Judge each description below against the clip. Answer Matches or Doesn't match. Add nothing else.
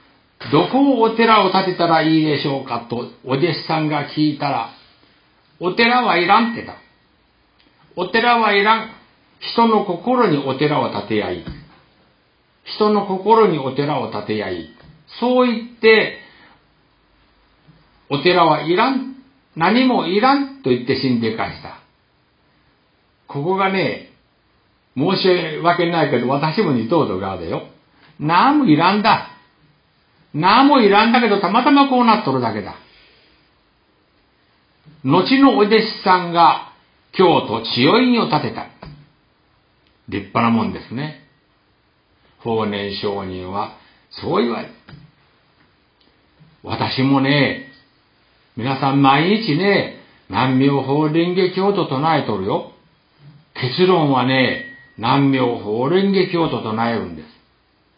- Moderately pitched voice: Matches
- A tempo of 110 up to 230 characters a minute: Matches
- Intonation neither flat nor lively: Doesn't match